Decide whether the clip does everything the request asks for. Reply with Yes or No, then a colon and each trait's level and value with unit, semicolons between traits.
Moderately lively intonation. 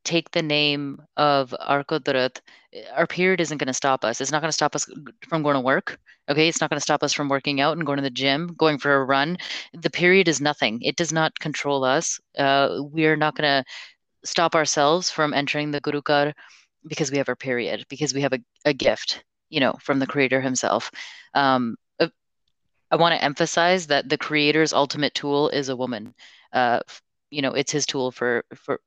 No: narrow, 2.3 semitones